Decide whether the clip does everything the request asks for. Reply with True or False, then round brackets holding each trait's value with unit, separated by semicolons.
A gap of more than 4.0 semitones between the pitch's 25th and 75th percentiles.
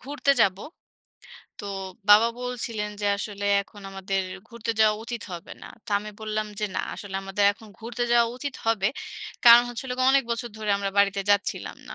False (2.8 semitones)